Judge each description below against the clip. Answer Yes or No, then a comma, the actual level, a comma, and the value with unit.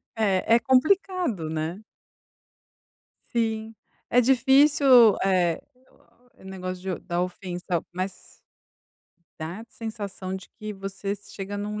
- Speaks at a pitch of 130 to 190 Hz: No, high, 200 Hz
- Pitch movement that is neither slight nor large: Yes, average, 3.8 semitones